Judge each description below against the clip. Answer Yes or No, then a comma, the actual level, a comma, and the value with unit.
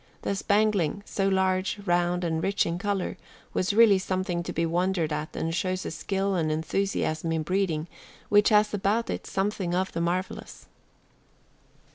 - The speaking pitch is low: No, medium, 185 Hz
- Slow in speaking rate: No, average, 160 wpm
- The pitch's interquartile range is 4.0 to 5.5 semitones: No, average, 2.8 semitones